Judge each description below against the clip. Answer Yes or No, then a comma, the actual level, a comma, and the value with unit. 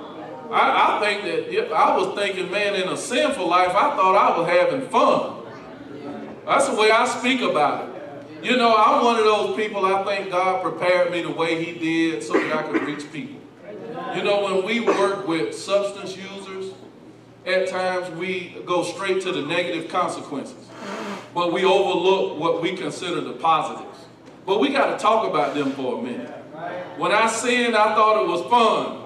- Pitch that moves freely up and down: No, average, 3.4 semitones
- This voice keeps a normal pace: Yes, average, 190 wpm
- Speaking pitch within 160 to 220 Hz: Yes, high, 190 Hz